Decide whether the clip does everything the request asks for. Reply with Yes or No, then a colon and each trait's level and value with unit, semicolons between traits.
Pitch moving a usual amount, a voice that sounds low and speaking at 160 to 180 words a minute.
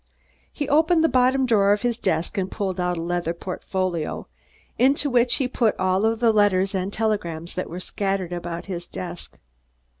No: average, 4.9 semitones; high, 195 Hz; average, 175 wpm